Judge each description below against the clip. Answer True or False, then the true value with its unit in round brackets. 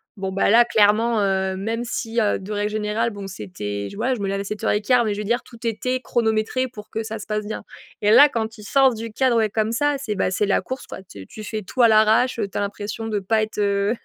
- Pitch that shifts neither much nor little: False (2.3 semitones)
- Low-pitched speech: False (215 Hz)